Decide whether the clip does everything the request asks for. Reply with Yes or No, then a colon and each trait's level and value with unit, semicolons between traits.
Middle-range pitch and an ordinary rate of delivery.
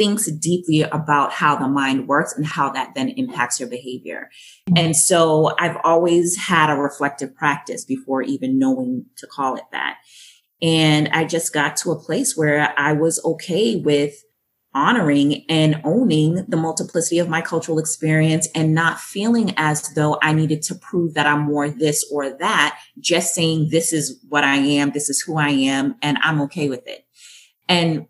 Yes: medium, 155 Hz; average, 175 wpm